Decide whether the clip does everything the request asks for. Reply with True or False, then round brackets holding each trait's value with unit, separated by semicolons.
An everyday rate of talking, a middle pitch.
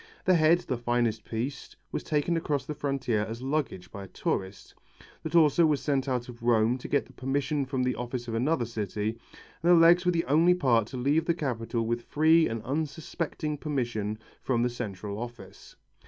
False (195 wpm; 130 Hz)